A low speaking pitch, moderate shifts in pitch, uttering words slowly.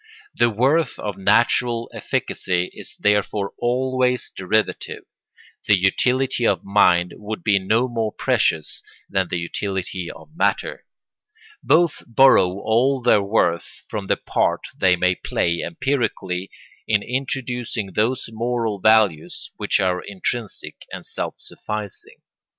Yes: low, 105 Hz; average, 4.4 semitones; slow, 120 wpm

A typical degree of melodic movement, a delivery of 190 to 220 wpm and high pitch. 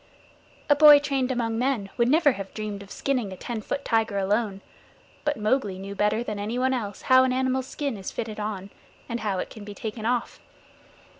Yes: average, 4.1 semitones; average, 200 wpm; high, 225 Hz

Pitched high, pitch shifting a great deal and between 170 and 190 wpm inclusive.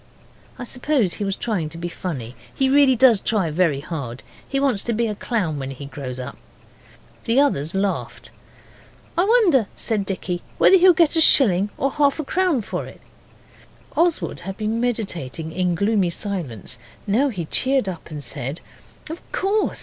Yes: high, 205 Hz; wide, 8.4 semitones; average, 175 wpm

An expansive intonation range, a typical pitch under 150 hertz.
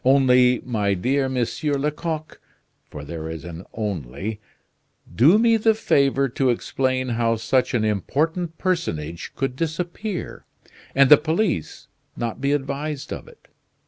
Yes: wide, 5.9 semitones; low, 135 Hz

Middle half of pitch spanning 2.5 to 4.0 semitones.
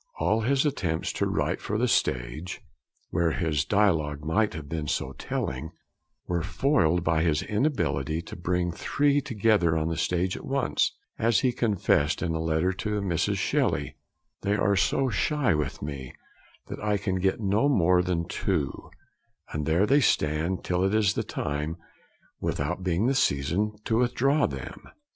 No: average, 5.2 semitones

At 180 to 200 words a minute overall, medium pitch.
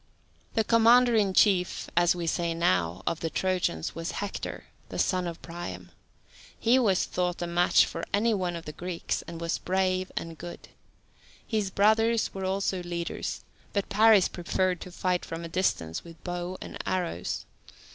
No: average, 165 wpm; medium, 180 Hz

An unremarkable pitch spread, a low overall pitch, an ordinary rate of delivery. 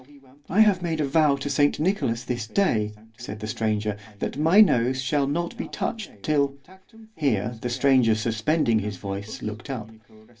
No: wide, 6.4 semitones; low, 130 Hz; average, 160 wpm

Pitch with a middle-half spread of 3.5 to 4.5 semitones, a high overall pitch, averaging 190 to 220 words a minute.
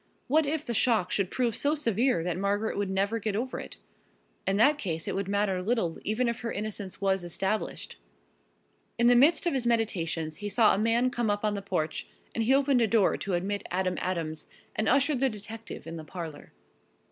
Yes: average, 4.1 semitones; high, 210 Hz; fast, 205 wpm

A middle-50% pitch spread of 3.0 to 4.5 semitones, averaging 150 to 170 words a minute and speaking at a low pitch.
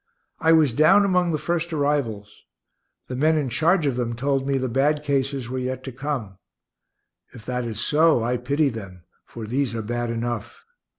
No: average, 4.2 semitones; average, 185 wpm; low, 130 Hz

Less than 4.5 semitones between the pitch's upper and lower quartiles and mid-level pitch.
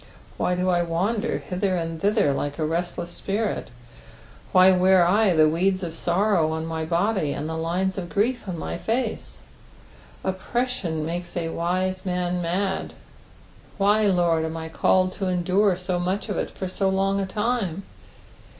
Yes: average, 2.7 semitones; medium, 180 Hz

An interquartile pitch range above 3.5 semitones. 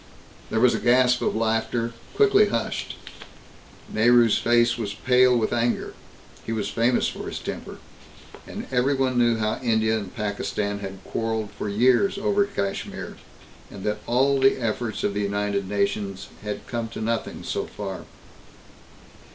No: average, 3.1 semitones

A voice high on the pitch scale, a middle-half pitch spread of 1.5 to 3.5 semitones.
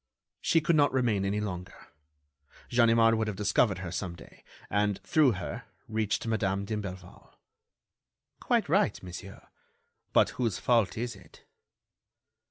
No: low, 105 Hz; average, 3.2 semitones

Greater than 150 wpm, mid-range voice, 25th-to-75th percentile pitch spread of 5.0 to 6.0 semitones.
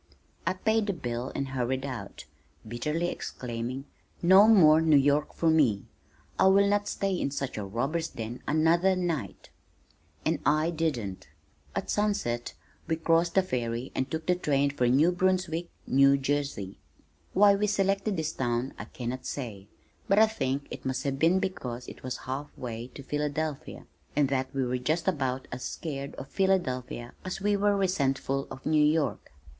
Yes: average, 170 wpm; medium, 145 Hz; wide, 5.4 semitones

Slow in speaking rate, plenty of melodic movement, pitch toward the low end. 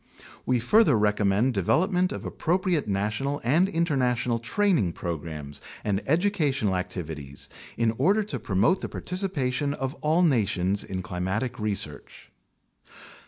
Yes: slow, 120 wpm; wide, 8.7 semitones; low, 125 Hz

